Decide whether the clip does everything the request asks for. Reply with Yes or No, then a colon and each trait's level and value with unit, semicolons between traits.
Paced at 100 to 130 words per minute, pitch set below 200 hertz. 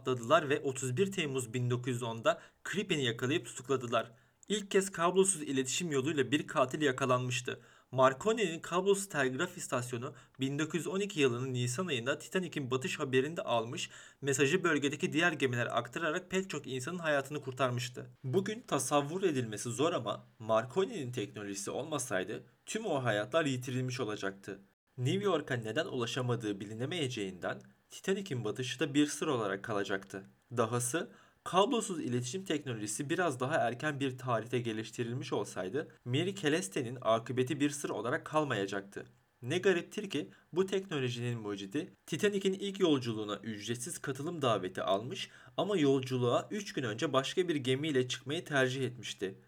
Yes: average, 125 wpm; low, 135 Hz